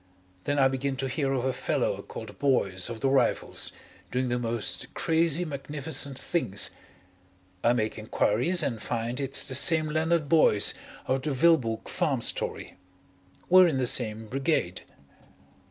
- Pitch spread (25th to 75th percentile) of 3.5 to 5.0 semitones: Yes, average, 4.5 semitones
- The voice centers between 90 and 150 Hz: Yes, low, 135 Hz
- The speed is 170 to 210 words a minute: No, average, 150 wpm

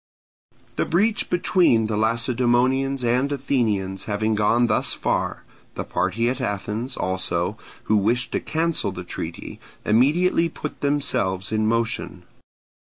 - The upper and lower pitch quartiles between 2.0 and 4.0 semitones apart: No, average, 4.4 semitones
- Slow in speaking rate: Yes, slow, 125 wpm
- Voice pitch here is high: No, low, 115 Hz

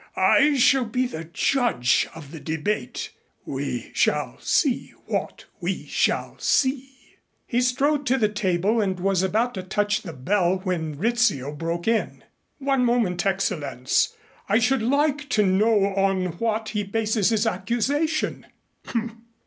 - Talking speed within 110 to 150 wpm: Yes, average, 140 wpm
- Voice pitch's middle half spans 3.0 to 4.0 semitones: No, average, 5.3 semitones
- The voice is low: No, high, 215 Hz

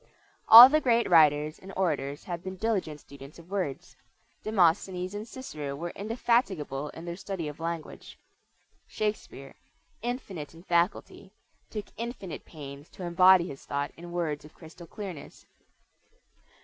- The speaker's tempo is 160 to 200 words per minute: No, slow, 135 wpm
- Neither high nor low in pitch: Yes, medium, 175 Hz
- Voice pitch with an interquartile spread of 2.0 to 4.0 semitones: No, average, 5.0 semitones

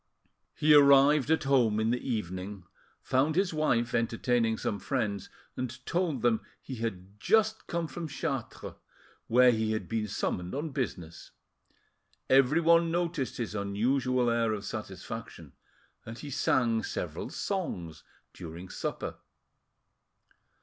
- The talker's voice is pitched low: Yes, low, 120 Hz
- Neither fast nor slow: No, slow, 125 wpm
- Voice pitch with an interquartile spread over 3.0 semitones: Yes, average, 5.1 semitones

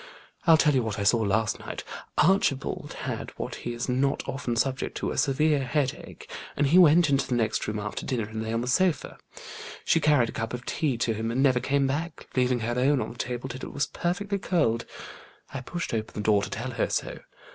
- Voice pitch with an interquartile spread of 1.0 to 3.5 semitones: No, average, 4.2 semitones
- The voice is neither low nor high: No, low, 130 Hz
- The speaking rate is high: Yes, fast, 225 wpm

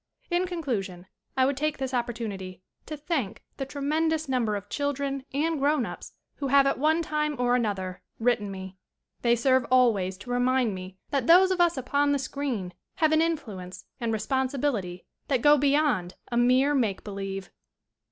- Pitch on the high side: Yes, very high, 255 Hz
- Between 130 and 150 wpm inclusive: No, average, 175 wpm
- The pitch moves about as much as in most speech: No, wide, 5.8 semitones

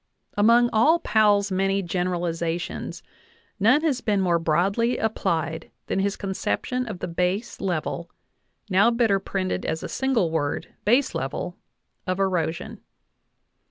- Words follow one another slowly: Yes, slow, 125 wpm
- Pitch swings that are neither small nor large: Yes, average, 4.4 semitones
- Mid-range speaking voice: No, high, 195 Hz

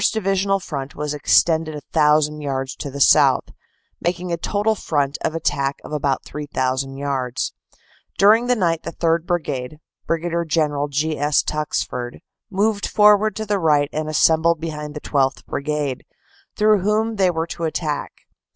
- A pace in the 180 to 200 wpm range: No, average, 155 wpm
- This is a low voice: No, medium, 155 Hz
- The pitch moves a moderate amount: Yes, average, 3.9 semitones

